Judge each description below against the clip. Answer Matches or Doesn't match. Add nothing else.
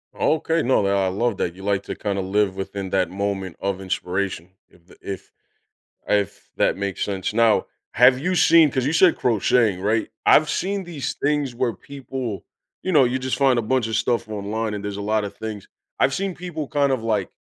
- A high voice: Doesn't match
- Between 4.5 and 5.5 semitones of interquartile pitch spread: Matches